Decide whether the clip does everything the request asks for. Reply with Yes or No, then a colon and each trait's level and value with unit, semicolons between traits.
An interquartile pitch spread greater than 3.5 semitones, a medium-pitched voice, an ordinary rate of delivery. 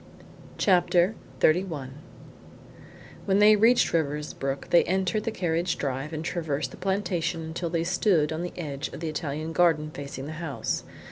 No: average, 3.2 semitones; medium, 165 Hz; average, 150 wpm